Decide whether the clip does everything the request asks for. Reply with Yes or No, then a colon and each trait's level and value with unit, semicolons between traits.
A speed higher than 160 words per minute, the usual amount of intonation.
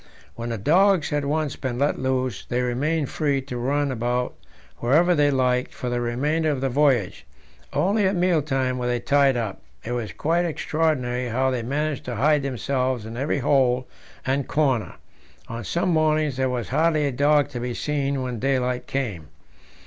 Yes: average, 180 wpm; average, 3.3 semitones